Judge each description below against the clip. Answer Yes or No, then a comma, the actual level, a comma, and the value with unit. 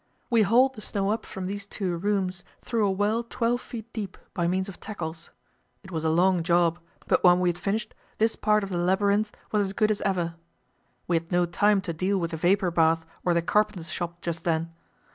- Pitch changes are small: No, average, 3.3 semitones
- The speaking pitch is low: No, high, 190 Hz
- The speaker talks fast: Yes, fast, 220 wpm